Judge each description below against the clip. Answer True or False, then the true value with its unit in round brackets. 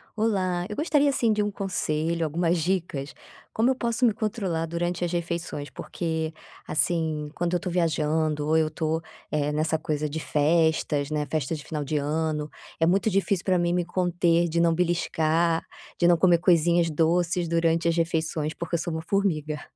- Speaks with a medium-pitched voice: True (165 Hz)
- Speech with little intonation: True (2.2 semitones)